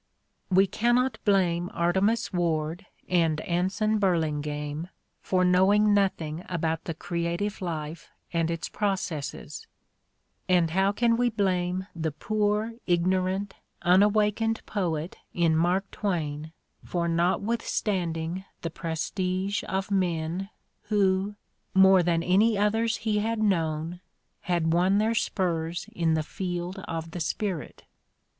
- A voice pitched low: No, medium, 180 Hz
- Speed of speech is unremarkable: No, slow, 120 wpm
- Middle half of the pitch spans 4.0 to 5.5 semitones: No, average, 3.4 semitones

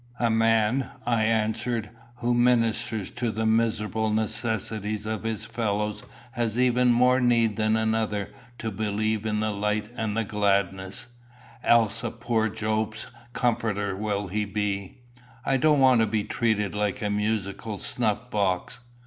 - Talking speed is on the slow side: No, average, 145 wpm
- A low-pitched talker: Yes, low, 110 Hz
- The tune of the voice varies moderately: No, narrow, 1.8 semitones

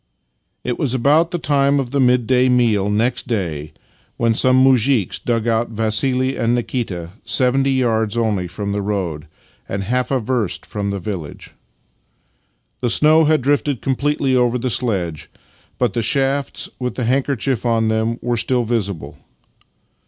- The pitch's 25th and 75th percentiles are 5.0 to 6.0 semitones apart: No, average, 3.7 semitones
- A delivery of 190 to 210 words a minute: No, average, 155 wpm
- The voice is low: Yes, low, 120 Hz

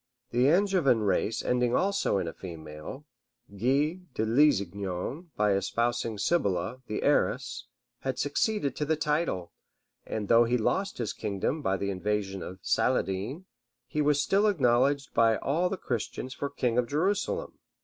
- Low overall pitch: Yes, low, 125 Hz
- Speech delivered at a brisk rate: No, average, 150 wpm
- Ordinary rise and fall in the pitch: No, wide, 6.7 semitones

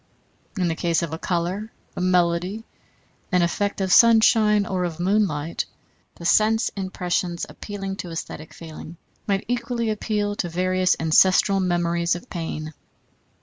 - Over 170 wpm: No, average, 140 wpm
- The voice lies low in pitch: No, medium, 185 Hz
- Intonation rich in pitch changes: No, average, 3.2 semitones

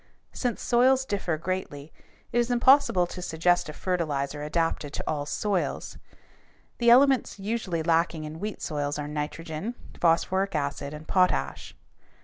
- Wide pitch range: Yes, wide, 5.7 semitones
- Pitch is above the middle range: No, medium, 175 Hz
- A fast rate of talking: No, slow, 135 wpm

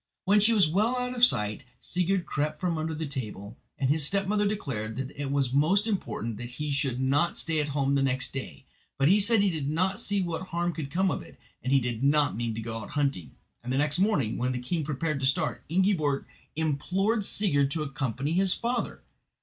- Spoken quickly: Yes, fast, 215 wpm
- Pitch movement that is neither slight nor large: No, wide, 5.9 semitones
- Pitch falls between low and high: Yes, medium, 150 Hz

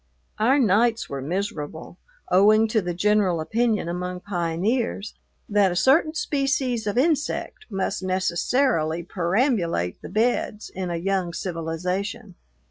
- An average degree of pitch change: Yes, average, 4.9 semitones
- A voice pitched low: No, high, 195 Hz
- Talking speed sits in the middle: No, slow, 125 wpm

